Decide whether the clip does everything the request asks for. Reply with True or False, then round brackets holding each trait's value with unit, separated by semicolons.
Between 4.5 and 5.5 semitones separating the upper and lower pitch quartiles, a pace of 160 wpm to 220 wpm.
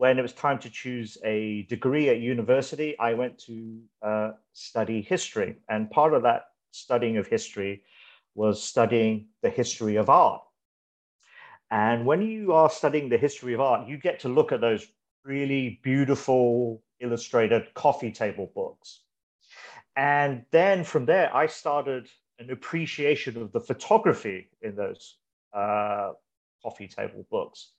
False (4.8 semitones; 145 wpm)